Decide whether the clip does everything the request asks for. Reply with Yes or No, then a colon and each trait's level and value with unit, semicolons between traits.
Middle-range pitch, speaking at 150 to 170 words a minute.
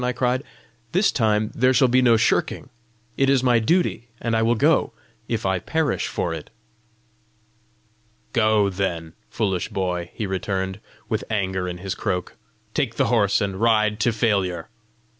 No: low, 110 Hz; average, 160 wpm